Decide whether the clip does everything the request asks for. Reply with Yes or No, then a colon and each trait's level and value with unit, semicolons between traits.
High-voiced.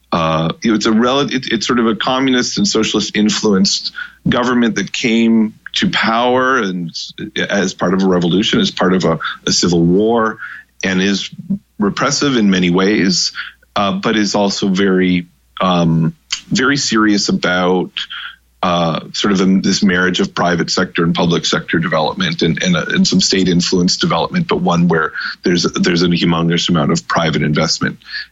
No: low, 105 Hz